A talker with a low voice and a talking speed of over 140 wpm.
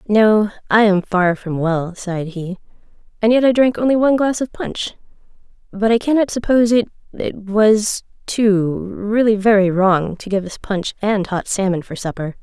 No: high, 205 Hz; average, 170 wpm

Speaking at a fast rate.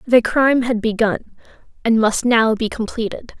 No: average, 160 wpm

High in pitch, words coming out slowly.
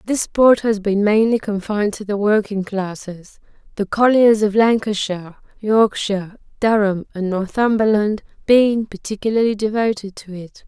Yes: high, 210 Hz; slow, 130 wpm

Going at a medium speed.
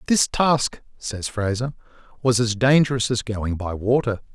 Yes: average, 150 wpm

